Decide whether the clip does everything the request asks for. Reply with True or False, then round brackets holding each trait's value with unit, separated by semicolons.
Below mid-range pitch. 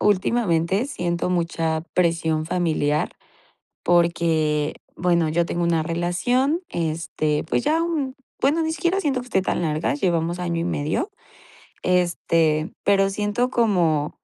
False (175 Hz)